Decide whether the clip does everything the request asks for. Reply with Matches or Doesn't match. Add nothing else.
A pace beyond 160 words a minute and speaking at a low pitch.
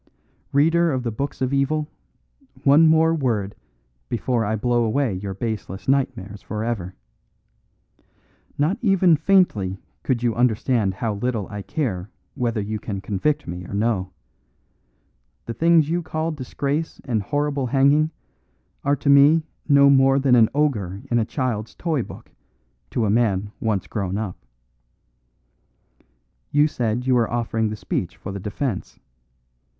Doesn't match